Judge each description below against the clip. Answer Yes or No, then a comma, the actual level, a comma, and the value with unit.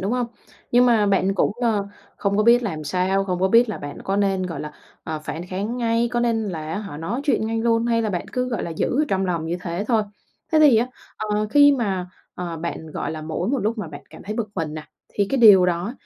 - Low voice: No, high, 200 Hz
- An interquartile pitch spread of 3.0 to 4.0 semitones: No, average, 4.8 semitones